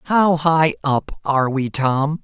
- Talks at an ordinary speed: Yes, average, 160 wpm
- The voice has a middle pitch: Yes, medium, 150 Hz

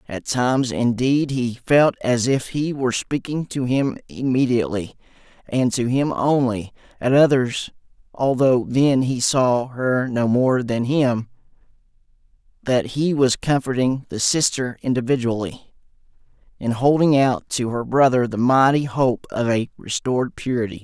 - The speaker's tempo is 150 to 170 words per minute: No, slow, 135 wpm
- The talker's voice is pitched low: Yes, low, 125 Hz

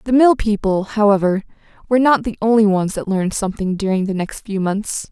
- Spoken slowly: No, average, 200 wpm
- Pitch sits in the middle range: No, high, 205 Hz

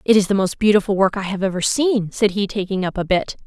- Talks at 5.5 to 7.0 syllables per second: Yes, 6.1 syllables/s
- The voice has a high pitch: Yes, high, 200 Hz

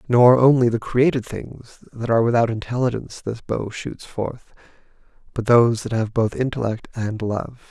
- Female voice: No, male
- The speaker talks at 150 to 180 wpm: Yes, average, 165 wpm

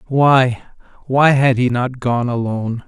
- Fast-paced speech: No, average, 145 wpm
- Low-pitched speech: Yes, low, 125 Hz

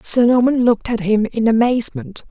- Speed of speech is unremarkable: Yes, average, 180 wpm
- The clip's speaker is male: No, female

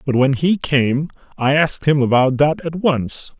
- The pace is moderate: Yes, average, 195 wpm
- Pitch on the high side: No, medium, 145 Hz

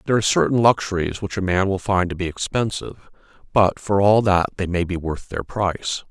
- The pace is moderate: No, fast, 215 wpm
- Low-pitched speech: Yes, very low, 95 Hz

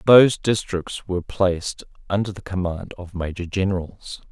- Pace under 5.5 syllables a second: Yes, 5.0 syllables/s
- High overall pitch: No, very low, 95 Hz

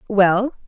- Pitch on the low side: No, high, 210 Hz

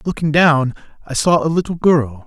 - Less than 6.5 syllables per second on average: Yes, 5.0 syllables/s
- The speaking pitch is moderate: Yes, medium, 150 Hz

